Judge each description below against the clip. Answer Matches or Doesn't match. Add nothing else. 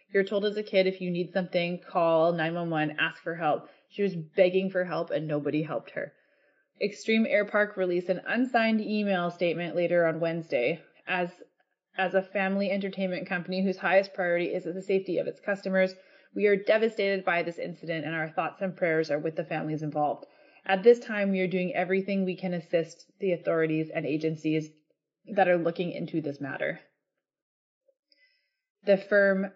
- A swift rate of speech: Doesn't match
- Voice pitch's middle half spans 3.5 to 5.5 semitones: Doesn't match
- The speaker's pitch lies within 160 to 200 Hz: Matches